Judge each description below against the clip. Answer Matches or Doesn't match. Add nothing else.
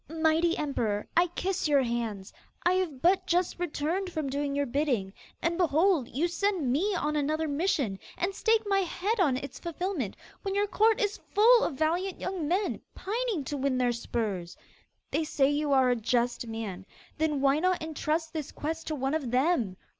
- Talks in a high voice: Matches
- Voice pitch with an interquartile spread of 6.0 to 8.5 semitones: Doesn't match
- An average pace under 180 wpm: Doesn't match